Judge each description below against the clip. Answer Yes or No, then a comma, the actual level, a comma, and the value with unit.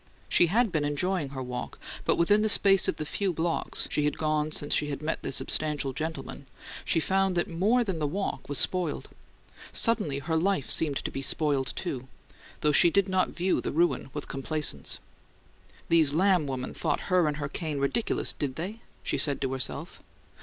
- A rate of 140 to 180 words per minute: No, average, 190 wpm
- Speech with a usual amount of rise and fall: Yes, average, 4.5 semitones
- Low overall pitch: No, medium, 155 Hz